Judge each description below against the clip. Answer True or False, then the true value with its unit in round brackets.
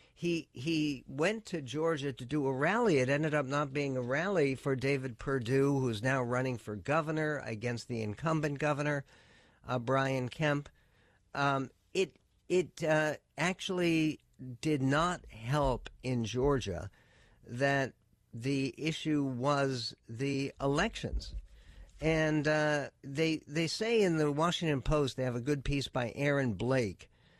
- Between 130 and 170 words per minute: True (140 wpm)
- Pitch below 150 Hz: True (140 Hz)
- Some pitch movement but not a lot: True (3.3 semitones)